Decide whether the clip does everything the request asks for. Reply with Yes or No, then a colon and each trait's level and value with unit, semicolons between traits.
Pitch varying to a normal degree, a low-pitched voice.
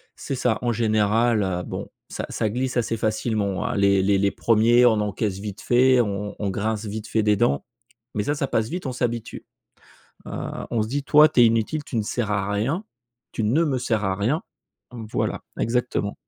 Yes: average, 3.1 semitones; low, 110 Hz